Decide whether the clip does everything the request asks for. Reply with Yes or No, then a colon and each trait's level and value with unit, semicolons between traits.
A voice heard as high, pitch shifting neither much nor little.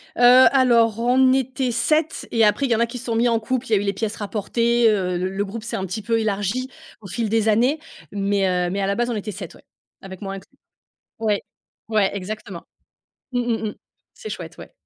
Yes: high, 225 Hz; average, 3.2 semitones